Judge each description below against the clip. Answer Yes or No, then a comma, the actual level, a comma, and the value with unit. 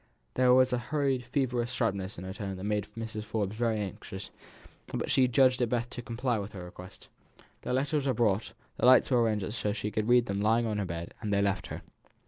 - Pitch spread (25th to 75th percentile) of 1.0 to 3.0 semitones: No, average, 3.6 semitones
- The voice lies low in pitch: Yes, low, 115 Hz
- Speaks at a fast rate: Yes, fast, 230 wpm